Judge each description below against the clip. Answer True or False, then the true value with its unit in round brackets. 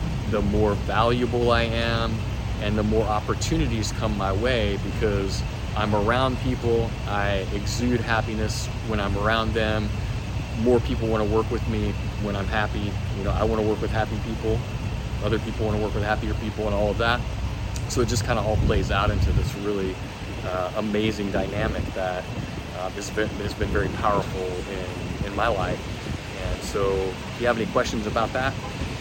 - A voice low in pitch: True (105 Hz)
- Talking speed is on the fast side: False (185 wpm)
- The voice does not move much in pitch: True (1.8 semitones)